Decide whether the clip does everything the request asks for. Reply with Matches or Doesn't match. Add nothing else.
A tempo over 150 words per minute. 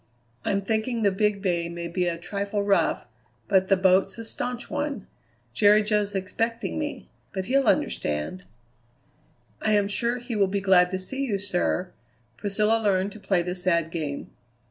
Matches